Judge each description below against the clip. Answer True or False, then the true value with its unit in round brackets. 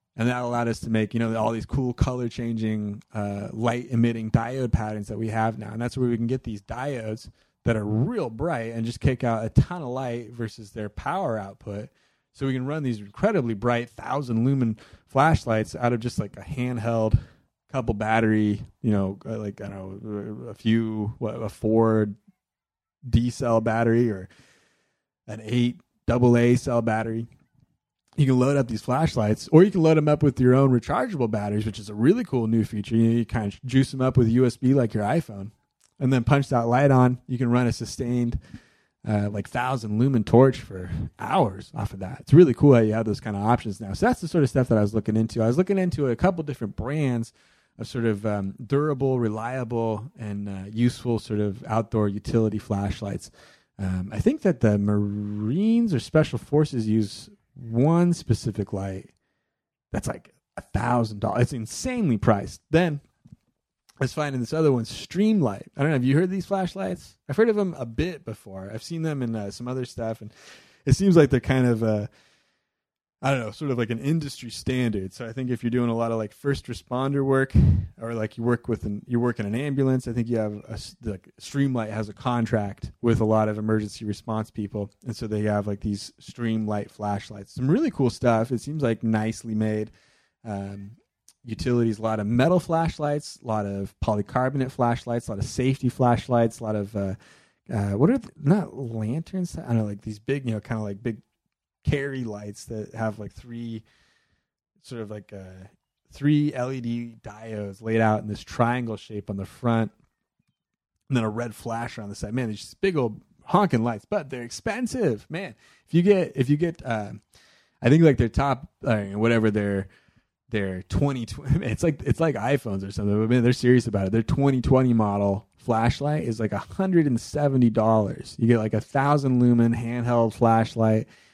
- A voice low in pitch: True (115 Hz)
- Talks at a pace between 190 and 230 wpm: True (200 wpm)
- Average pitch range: True (3.4 semitones)